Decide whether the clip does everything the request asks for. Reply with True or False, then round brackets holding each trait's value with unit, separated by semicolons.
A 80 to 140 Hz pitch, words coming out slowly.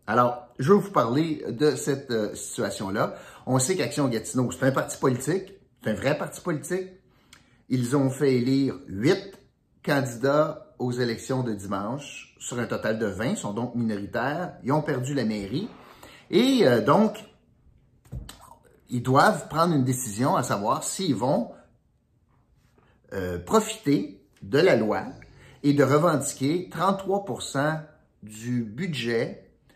True (135 Hz; 140 wpm)